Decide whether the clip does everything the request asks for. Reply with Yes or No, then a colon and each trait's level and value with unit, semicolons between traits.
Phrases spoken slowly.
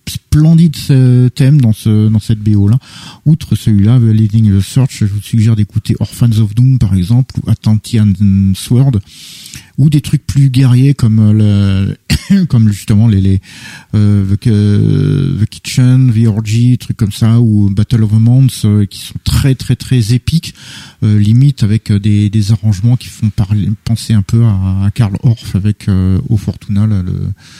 No: average, 175 wpm